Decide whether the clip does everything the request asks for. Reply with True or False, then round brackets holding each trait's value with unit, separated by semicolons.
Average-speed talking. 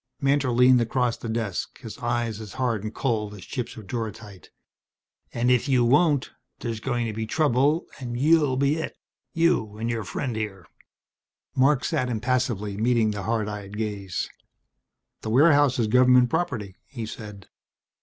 True (160 wpm)